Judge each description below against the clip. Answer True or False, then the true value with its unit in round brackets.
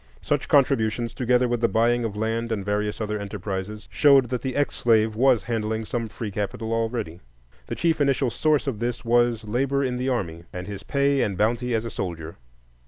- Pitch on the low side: True (115 Hz)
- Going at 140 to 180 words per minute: False (195 wpm)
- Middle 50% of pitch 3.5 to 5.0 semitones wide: False (2.9 semitones)